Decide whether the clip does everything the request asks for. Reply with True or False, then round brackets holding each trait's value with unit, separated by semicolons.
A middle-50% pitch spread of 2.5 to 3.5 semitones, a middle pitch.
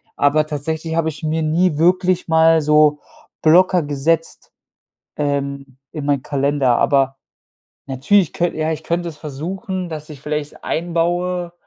True (2.9 semitones; 155 Hz)